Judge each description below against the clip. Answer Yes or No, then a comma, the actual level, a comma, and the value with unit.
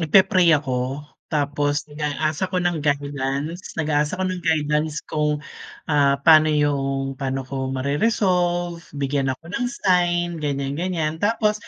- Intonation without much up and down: No, average, 3.7 semitones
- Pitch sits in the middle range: Yes, medium, 150 Hz